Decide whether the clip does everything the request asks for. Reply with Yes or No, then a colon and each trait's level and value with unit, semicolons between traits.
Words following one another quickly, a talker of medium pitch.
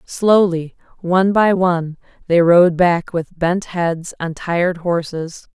No: average, 140 wpm; medium, 175 Hz